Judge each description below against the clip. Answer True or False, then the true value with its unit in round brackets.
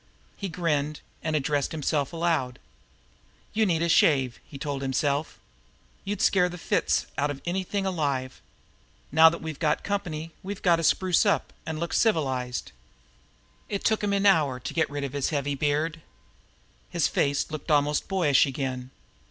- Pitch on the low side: False (155 Hz)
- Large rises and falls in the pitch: False (3.6 semitones)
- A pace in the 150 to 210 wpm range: True (160 wpm)